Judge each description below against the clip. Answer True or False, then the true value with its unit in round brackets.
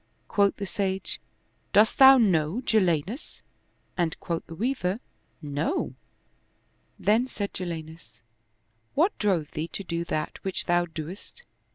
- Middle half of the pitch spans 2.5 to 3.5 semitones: False (4.7 semitones)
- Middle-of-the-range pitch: True (180 Hz)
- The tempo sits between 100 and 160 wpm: True (145 wpm)